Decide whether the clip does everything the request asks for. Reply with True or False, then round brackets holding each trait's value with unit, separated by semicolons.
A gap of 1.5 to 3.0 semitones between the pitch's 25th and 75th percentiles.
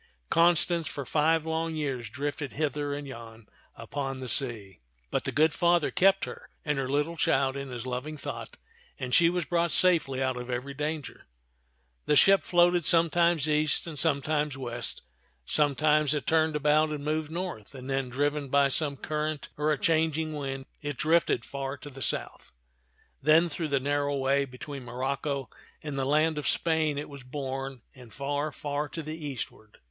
True (2.6 semitones)